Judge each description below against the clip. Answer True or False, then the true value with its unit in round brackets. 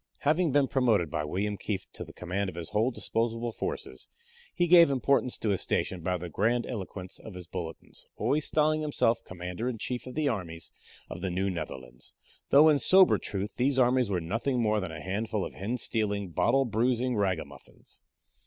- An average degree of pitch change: False (5.7 semitones)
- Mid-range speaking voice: False (110 Hz)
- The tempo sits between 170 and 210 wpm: True (185 wpm)